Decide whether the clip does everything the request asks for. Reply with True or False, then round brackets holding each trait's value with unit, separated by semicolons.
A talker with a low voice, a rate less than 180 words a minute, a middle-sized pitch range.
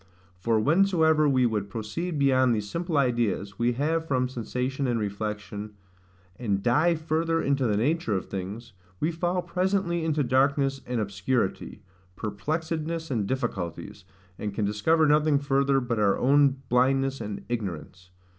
False (130 Hz; 145 wpm; 6.3 semitones)